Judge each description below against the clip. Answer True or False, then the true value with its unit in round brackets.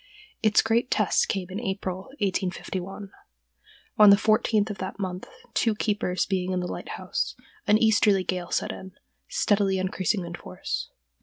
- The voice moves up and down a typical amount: False (2.2 semitones)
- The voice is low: False (195 Hz)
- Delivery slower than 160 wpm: True (150 wpm)